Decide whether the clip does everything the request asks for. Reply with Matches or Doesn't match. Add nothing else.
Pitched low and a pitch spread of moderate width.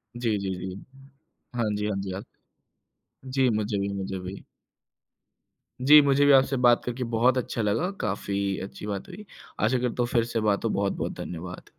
Matches